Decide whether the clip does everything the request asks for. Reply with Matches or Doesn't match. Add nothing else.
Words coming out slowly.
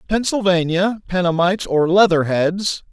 Matches